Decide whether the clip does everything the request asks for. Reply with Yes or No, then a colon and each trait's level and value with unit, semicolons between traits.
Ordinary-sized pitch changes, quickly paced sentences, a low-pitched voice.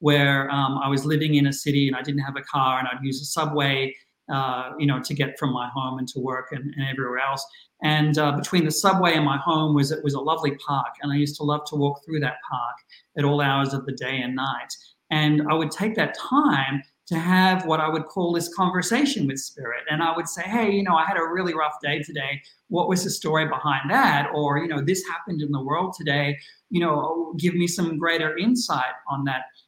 No: average, 3.2 semitones; fast, 245 wpm; medium, 150 Hz